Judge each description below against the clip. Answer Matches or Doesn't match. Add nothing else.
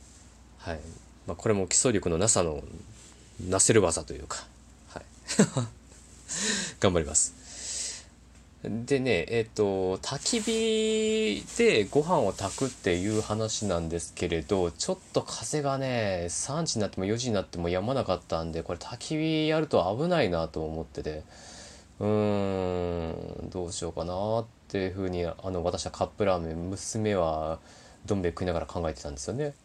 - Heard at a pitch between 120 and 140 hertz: Doesn't match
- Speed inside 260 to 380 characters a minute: Matches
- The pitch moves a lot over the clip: Matches